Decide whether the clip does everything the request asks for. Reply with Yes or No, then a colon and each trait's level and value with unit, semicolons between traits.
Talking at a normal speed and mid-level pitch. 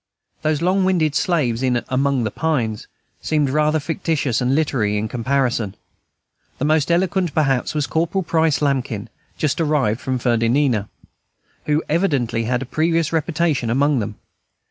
Yes: average, 145 wpm; medium, 145 Hz